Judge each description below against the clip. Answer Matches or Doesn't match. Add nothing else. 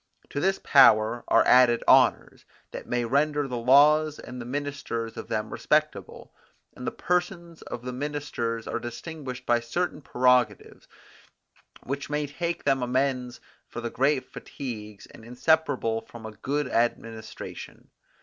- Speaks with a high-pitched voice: Doesn't match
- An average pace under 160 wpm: Matches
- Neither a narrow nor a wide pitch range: Matches